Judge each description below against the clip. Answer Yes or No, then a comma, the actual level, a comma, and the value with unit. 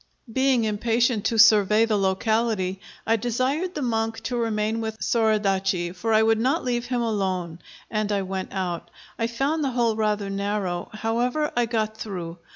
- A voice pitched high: Yes, high, 220 Hz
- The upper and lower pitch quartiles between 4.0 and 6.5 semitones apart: No, average, 3.0 semitones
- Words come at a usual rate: Yes, average, 165 wpm